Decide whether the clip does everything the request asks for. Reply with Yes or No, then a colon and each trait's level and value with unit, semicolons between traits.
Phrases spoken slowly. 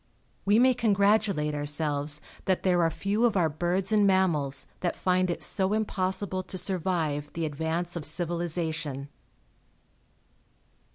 Yes: slow, 130 wpm